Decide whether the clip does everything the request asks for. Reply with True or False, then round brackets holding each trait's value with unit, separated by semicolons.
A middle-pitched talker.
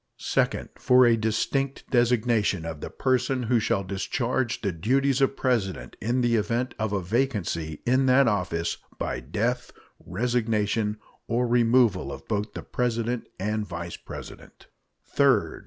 False (115 Hz)